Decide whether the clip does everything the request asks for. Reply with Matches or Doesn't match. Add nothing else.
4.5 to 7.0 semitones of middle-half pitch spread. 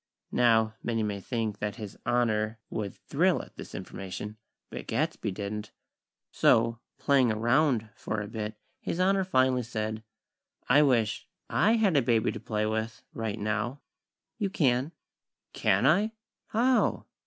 Doesn't match